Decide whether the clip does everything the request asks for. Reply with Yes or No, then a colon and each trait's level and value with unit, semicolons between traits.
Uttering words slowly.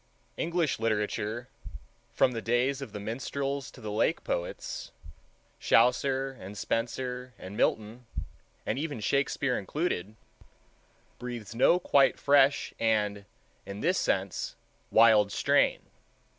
Yes: slow, 105 wpm